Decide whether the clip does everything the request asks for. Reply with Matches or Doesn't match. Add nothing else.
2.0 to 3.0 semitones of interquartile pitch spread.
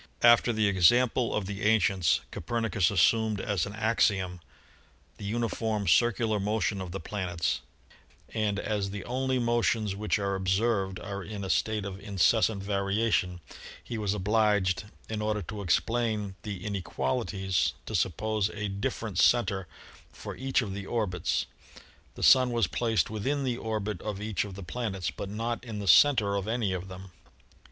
Matches